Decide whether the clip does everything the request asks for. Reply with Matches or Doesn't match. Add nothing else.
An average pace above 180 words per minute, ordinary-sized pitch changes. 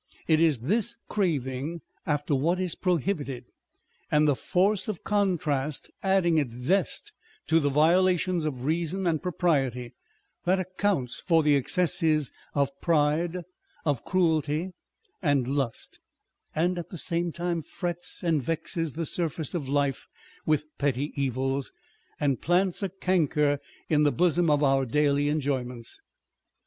Doesn't match